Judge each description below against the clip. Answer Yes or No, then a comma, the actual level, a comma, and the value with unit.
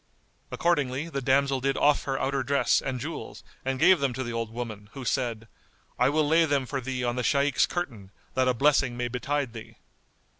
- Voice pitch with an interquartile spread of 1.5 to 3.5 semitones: Yes, average, 2.7 semitones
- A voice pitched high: No, low, 135 Hz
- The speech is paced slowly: No, average, 200 wpm